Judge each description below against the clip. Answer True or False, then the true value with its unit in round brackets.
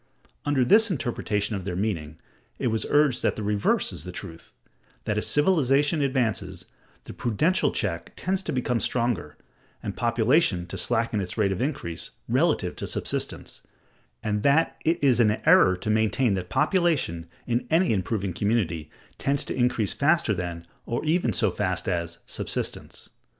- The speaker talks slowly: False (160 wpm)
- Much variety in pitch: True (6.7 semitones)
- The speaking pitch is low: True (115 Hz)